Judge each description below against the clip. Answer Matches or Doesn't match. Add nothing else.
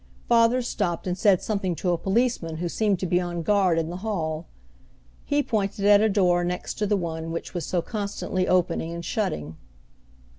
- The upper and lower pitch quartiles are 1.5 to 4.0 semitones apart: Matches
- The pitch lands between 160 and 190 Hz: Matches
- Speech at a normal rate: Matches